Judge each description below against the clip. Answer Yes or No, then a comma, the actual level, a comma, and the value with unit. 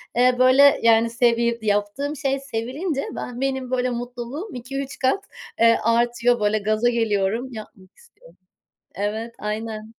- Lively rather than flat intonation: No, average, 2.9 semitones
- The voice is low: No, high, 240 Hz